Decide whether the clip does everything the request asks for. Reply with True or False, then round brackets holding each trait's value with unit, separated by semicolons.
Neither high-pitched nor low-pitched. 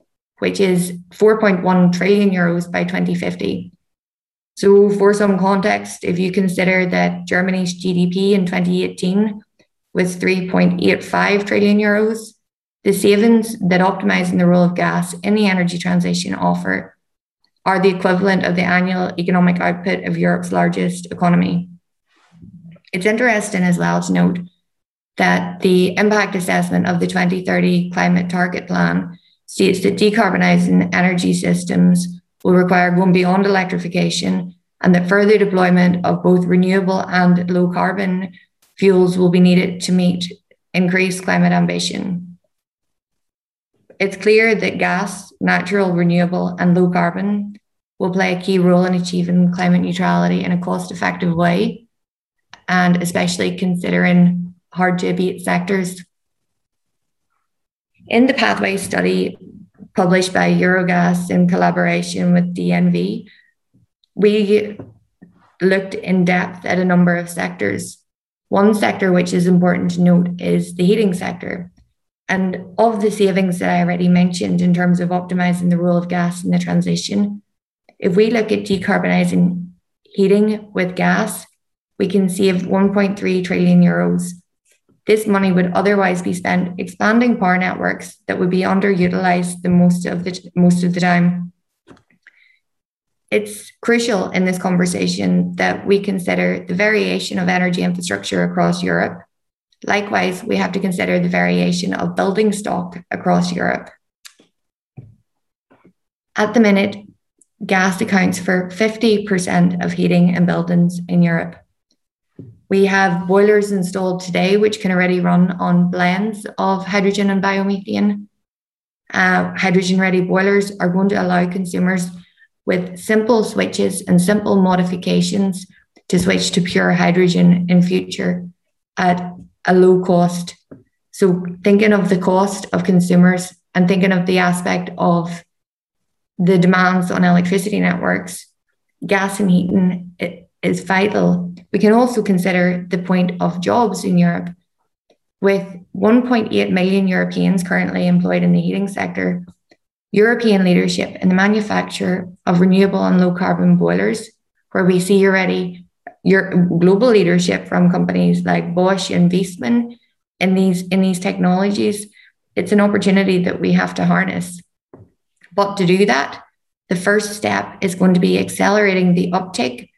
True (180 Hz)